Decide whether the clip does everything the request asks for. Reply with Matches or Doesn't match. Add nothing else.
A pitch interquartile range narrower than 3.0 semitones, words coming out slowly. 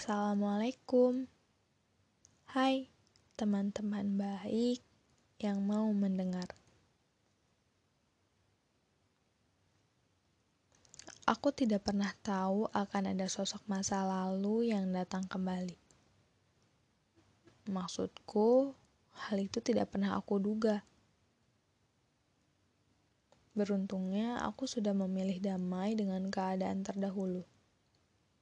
Matches